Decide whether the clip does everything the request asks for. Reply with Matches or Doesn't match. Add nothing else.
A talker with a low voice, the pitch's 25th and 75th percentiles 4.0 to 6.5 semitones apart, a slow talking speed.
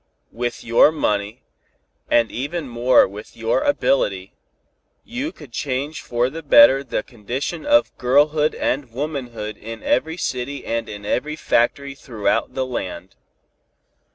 Matches